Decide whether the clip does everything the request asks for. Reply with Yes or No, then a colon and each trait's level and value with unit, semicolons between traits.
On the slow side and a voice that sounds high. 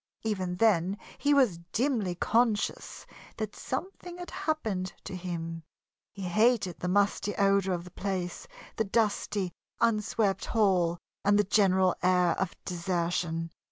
Yes: slow, 130 wpm; high, 195 Hz